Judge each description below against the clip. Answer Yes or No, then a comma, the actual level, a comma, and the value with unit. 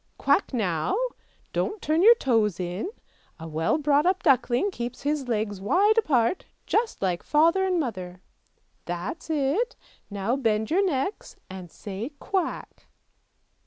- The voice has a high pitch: Yes, very high, 260 Hz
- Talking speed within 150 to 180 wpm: No, slow, 135 wpm